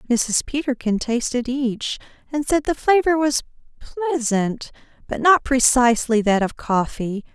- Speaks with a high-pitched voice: Yes, very high, 255 Hz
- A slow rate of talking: Yes, slow, 130 wpm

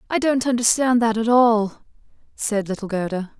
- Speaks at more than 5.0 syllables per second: No, 4.9 syllables/s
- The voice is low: No, high, 225 Hz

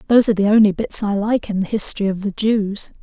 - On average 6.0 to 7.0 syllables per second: Yes, 6.5 syllables/s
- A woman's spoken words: Yes, female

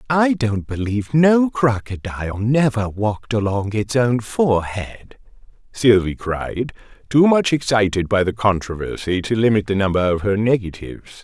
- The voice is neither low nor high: No, low, 110 Hz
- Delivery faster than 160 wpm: No, average, 140 wpm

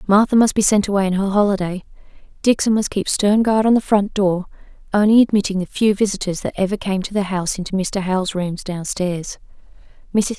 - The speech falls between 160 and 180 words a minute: No, average, 195 wpm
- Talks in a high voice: Yes, high, 200 Hz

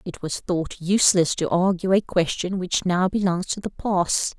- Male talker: No, female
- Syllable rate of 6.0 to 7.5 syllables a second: No, 4.5 syllables/s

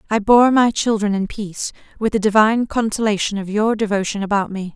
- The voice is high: Yes, high, 210 Hz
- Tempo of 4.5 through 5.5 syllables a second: No, 5.8 syllables/s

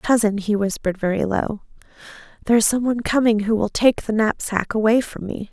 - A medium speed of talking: Yes, average, 185 wpm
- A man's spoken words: No, female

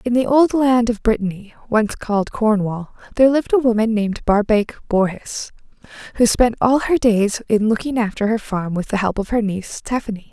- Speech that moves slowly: No, average, 190 wpm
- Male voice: No, female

